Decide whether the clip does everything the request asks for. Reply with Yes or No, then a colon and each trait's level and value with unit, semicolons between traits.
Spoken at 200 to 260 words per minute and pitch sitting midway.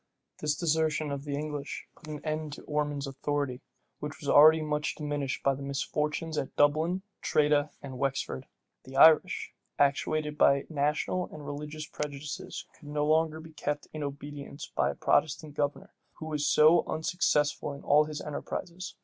No: average, 160 wpm; medium, 150 Hz